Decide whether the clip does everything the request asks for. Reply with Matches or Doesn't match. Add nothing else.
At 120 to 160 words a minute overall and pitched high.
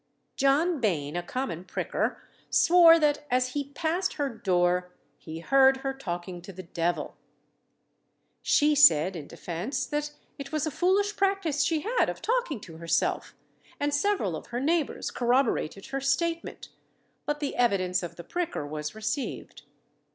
Matches